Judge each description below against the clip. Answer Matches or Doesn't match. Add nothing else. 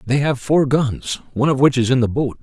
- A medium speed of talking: Doesn't match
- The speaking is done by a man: Matches